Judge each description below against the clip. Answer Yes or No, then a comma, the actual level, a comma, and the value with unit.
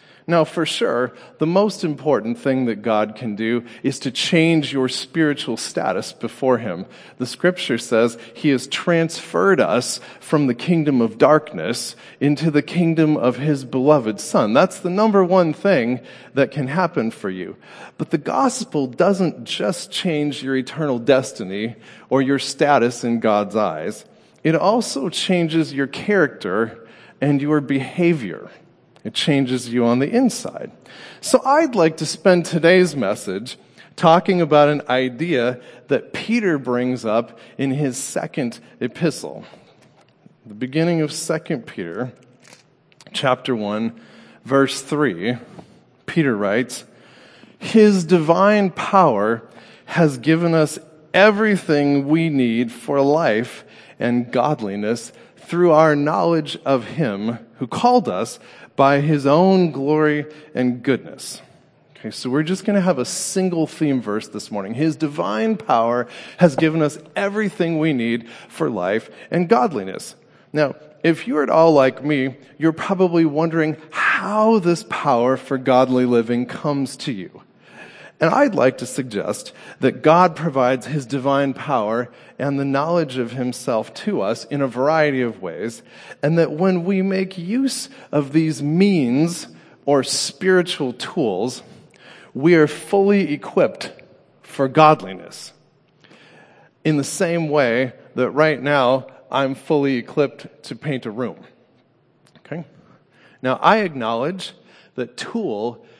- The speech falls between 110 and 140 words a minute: Yes, slow, 135 wpm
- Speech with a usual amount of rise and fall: Yes, average, 4.9 semitones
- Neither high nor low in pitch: Yes, medium, 150 Hz